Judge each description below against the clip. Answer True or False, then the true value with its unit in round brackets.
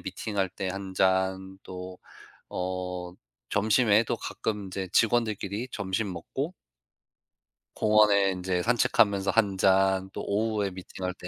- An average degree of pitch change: False (2.2 semitones)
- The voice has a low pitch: True (95 Hz)